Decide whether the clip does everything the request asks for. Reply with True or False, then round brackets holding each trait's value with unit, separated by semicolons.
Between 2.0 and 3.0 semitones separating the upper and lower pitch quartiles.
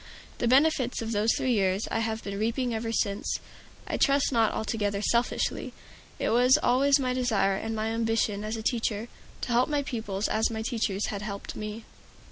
True (2.5 semitones)